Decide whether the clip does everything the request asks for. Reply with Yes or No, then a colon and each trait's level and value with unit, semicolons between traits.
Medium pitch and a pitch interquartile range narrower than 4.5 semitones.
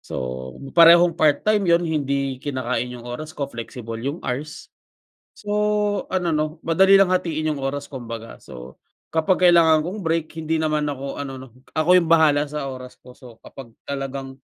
Yes: medium, 150 Hz; average, 4.1 semitones